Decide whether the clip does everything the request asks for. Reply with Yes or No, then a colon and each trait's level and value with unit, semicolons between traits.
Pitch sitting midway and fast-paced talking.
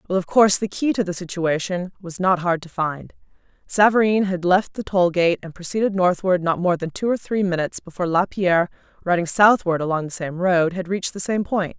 Yes: medium, 180 Hz; fast, 215 wpm